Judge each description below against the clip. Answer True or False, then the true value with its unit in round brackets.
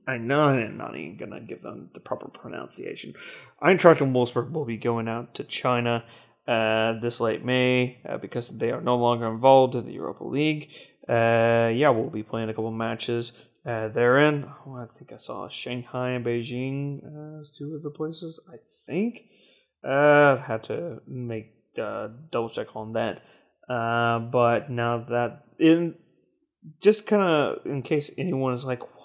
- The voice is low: True (125 Hz)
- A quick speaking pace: False (175 wpm)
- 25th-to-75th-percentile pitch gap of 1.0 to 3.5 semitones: False (4.0 semitones)